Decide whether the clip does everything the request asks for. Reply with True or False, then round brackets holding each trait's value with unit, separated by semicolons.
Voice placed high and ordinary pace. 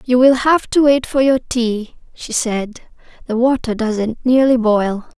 True (240 Hz; 175 wpm)